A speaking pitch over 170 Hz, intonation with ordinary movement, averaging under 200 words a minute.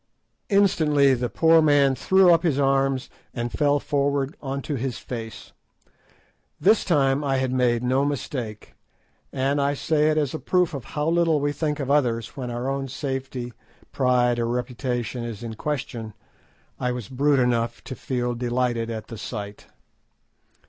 No: low, 135 Hz; average, 3.1 semitones; average, 155 wpm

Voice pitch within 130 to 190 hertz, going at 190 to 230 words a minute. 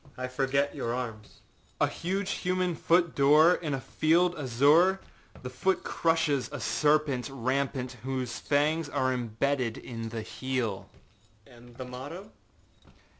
No: low, 135 Hz; slow, 135 wpm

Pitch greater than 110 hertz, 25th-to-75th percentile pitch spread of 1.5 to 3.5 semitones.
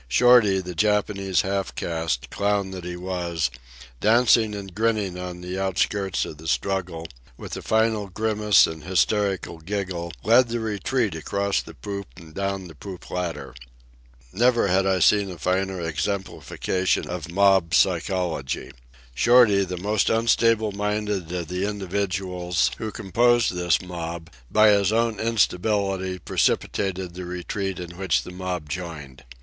No: very low, 95 Hz; average, 2.8 semitones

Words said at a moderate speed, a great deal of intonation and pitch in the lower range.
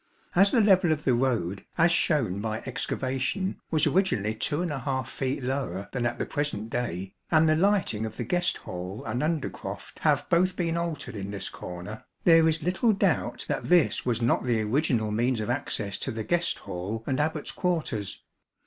Yes: average, 180 wpm; wide, 7.2 semitones; low, 130 Hz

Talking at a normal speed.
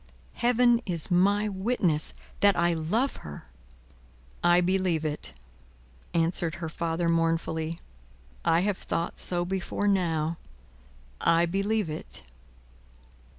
No: slow, 110 wpm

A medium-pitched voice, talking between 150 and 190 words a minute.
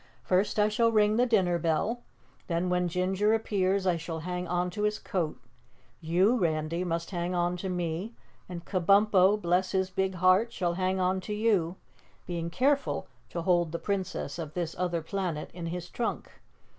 Yes: medium, 180 Hz; average, 175 wpm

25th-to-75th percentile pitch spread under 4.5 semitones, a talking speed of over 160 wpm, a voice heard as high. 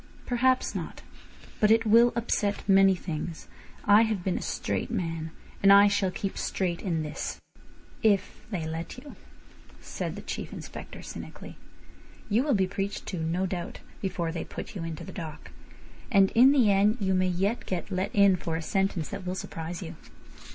Yes: average, 3.3 semitones; average, 180 wpm; high, 195 Hz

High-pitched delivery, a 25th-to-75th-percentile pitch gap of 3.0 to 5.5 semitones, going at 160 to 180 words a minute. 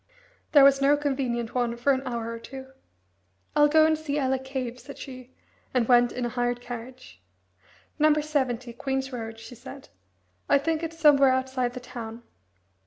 No: very high, 260 Hz; narrow, 2.6 semitones; average, 175 wpm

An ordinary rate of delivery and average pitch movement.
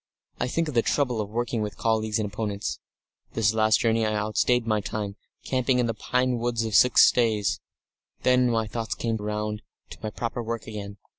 No: average, 195 wpm; narrow, 2.2 semitones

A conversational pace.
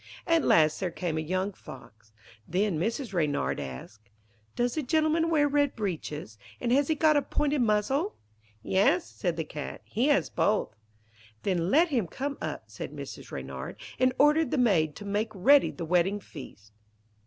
Yes: average, 170 wpm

